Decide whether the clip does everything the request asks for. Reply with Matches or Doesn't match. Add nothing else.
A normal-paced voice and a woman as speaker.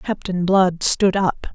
Matches